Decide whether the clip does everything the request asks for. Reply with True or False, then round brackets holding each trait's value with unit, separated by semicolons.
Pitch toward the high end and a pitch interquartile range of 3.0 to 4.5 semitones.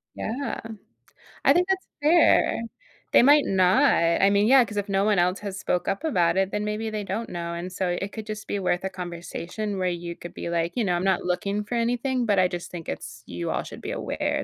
True (195 Hz; 3.9 semitones)